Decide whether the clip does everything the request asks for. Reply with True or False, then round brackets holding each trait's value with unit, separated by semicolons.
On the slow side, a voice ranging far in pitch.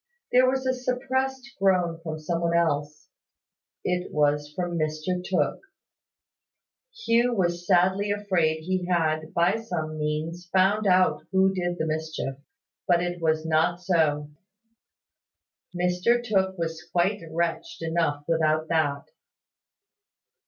False (125 wpm; 3.2 semitones)